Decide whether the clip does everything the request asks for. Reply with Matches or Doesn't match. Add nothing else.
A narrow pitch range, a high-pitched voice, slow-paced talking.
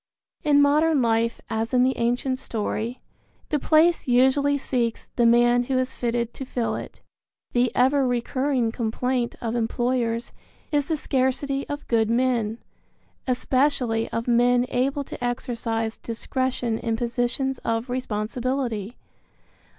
Matches